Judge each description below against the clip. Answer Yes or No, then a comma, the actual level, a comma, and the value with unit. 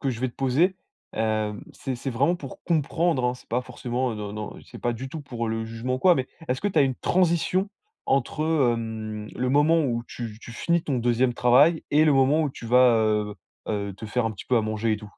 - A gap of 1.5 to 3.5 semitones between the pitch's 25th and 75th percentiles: No, average, 4.3 semitones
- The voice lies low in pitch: Yes, low, 125 Hz